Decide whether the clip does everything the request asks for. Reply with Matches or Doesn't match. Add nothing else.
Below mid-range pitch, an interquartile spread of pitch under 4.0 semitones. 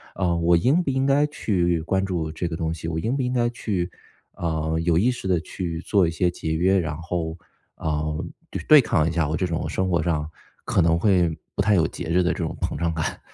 Matches